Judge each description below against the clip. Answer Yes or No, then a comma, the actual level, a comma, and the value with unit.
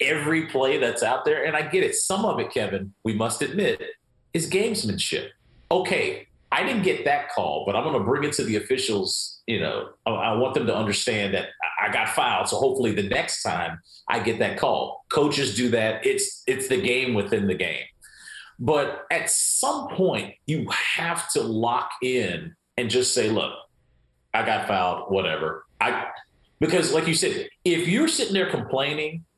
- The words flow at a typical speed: Yes, average, 185 wpm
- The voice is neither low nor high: Yes, medium, 155 Hz